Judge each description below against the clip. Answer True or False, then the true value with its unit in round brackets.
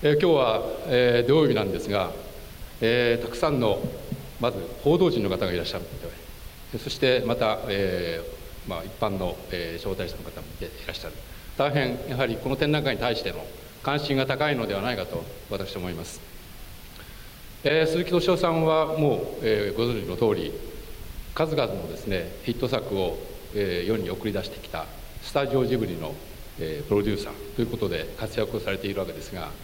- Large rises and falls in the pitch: True (5.8 semitones)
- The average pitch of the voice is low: True (120 Hz)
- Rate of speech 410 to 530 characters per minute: False (350 characters per minute)